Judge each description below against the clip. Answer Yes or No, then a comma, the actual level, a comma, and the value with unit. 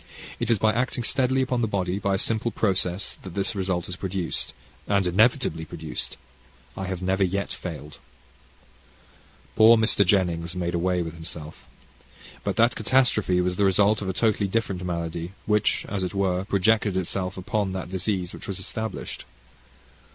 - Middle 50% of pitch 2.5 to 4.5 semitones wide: Yes, average, 3.0 semitones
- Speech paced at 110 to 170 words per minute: Yes, average, 165 wpm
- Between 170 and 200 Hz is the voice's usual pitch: No, very low, 95 Hz